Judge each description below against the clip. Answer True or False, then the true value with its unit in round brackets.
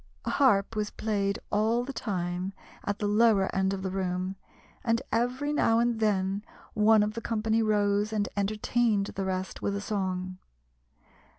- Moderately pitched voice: False (205 Hz)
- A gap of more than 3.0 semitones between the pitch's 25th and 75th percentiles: False (2.5 semitones)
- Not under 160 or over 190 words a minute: True (165 wpm)